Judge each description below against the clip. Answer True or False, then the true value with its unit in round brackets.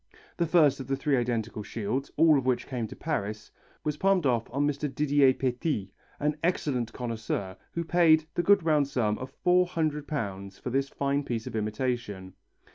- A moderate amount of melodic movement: True (4.8 semitones)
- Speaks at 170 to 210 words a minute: True (175 wpm)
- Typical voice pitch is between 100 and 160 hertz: True (135 Hz)